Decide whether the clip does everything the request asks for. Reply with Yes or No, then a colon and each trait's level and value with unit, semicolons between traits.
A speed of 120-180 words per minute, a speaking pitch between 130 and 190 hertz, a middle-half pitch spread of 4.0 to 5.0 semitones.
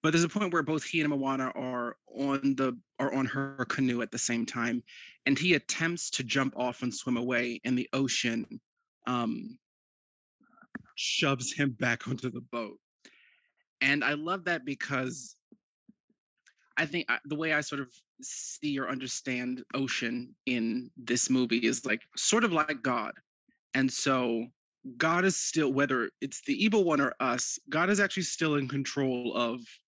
Yes: average, 165 wpm; low, 135 Hz; average, 4.4 semitones